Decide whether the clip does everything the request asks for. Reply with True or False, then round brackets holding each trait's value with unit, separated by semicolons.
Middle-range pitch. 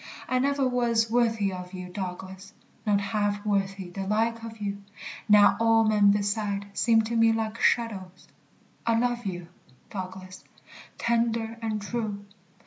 False (210 Hz)